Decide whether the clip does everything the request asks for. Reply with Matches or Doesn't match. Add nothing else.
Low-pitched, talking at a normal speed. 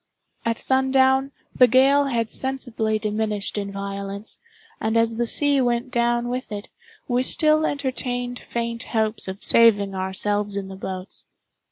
Doesn't match